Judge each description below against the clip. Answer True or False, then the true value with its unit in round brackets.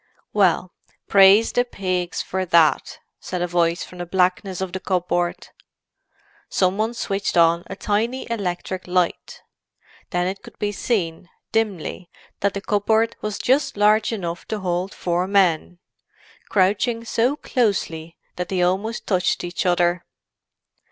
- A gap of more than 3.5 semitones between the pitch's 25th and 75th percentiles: False (2.9 semitones)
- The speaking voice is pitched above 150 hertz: True (190 Hz)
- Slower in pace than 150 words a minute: True (140 wpm)